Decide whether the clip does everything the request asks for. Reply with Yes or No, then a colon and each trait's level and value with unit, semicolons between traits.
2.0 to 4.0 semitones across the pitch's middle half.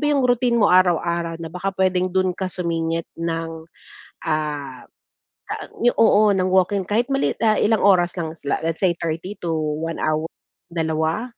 Yes: average, 2.8 semitones